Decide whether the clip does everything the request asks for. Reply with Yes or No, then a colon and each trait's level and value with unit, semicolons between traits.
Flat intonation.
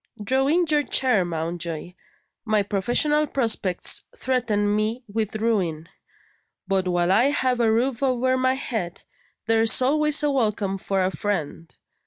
No: average, 5.2 semitones